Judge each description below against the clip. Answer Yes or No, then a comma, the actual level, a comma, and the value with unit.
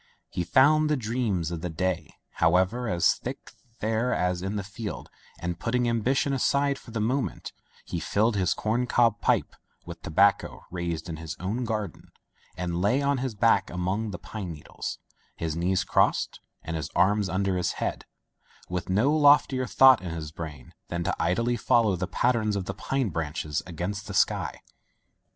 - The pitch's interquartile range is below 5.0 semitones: No, wide, 5.5 semitones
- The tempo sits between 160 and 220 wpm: Yes, average, 175 wpm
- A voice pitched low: Yes, low, 100 Hz